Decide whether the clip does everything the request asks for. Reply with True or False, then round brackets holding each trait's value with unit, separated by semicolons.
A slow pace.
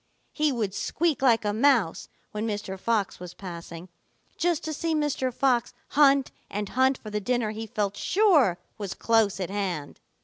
False (170 wpm)